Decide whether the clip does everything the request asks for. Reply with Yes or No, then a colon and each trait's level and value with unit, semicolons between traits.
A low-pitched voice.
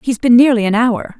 No: high, 235 Hz